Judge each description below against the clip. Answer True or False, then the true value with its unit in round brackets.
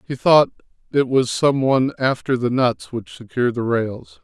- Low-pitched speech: True (125 Hz)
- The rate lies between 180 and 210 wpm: True (185 wpm)